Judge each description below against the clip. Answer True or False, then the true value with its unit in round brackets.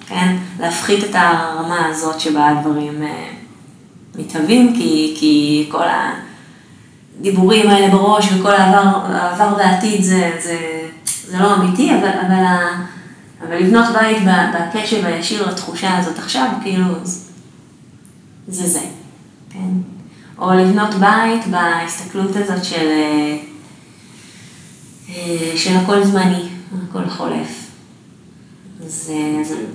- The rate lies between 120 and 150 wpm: False (100 wpm)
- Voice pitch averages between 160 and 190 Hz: True (185 Hz)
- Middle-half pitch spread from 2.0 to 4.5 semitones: True (3.1 semitones)